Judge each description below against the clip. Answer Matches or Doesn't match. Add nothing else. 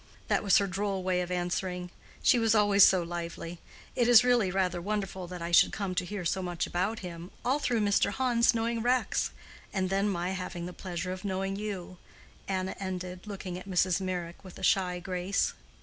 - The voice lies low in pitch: Doesn't match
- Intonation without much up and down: Matches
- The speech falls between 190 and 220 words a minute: Matches